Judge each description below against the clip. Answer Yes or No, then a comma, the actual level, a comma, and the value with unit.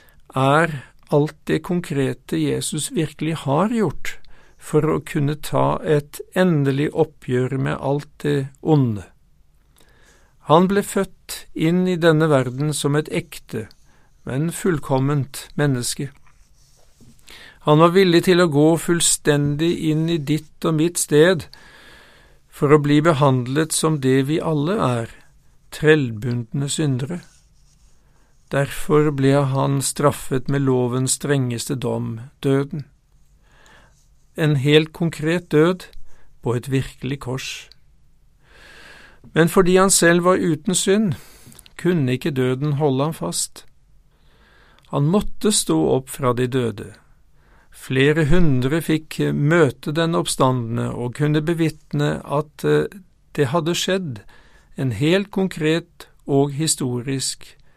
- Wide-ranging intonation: No, average, 3.5 semitones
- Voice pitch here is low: No, medium, 150 Hz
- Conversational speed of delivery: No, slow, 115 wpm